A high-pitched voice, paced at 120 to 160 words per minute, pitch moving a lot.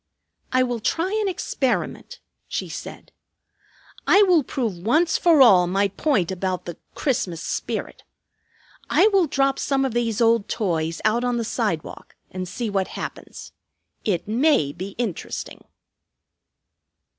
Yes: high, 230 Hz; slow, 135 wpm; wide, 6.4 semitones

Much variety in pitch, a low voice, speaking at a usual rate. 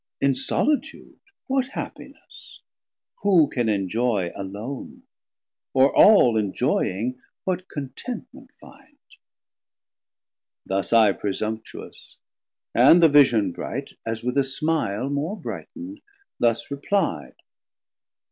No: wide, 7.0 semitones; low, 130 Hz; slow, 95 wpm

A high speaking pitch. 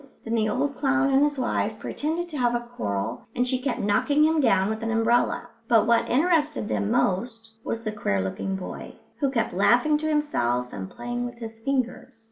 Yes: high, 240 Hz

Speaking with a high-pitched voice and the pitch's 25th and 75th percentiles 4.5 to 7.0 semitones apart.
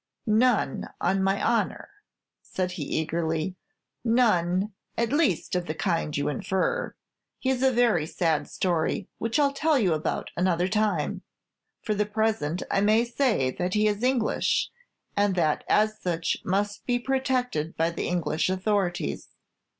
Yes: high, 195 Hz; average, 5.1 semitones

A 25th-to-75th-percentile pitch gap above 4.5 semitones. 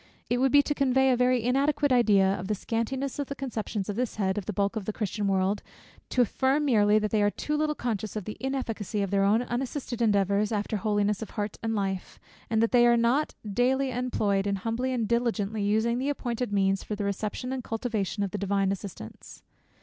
No: average, 3.7 semitones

